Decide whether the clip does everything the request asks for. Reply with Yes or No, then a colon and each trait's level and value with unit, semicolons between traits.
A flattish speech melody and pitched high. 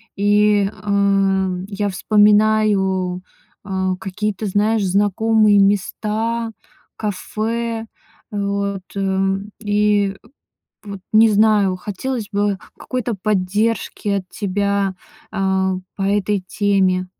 Yes: narrow, 1.7 semitones; high, 205 Hz